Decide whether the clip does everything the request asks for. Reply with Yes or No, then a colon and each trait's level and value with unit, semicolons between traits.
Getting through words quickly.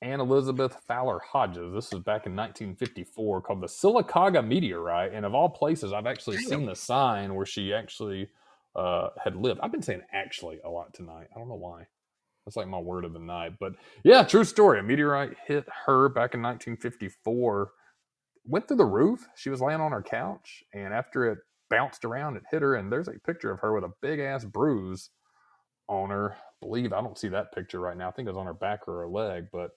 Yes: fast, 220 wpm